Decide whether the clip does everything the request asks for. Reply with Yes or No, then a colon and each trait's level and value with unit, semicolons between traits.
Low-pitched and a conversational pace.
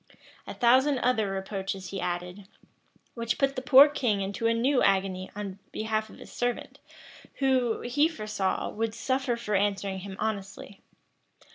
No: high, 215 Hz; average, 150 wpm